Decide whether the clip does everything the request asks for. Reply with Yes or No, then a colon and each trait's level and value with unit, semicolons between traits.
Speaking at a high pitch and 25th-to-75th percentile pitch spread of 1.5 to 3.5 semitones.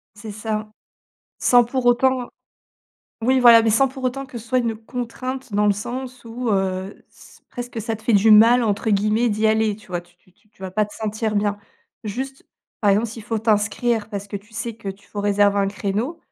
Yes: high, 220 Hz; average, 2.9 semitones